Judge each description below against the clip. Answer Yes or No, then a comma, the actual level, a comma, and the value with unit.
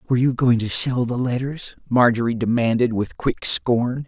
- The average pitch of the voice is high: No, low, 120 Hz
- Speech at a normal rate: Yes, average, 175 wpm